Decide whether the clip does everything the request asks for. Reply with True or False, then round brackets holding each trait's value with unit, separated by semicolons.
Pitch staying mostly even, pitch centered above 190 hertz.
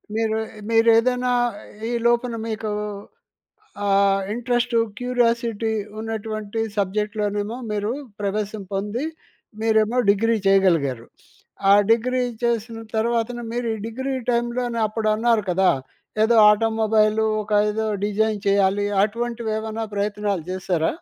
True (2.2 semitones; 220 Hz)